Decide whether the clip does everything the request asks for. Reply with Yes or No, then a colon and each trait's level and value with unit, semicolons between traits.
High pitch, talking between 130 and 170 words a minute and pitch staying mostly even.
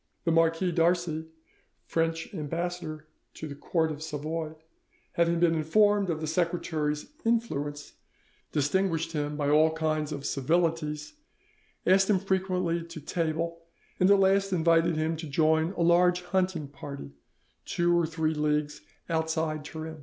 No: medium, 165 Hz; average, 140 wpm; narrow, 2.1 semitones